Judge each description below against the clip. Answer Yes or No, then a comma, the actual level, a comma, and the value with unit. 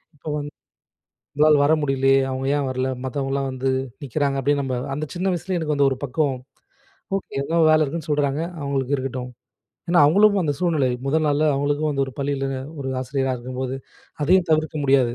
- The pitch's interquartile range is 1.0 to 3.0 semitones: Yes, narrow, 2.5 semitones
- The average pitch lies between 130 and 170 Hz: Yes, medium, 140 Hz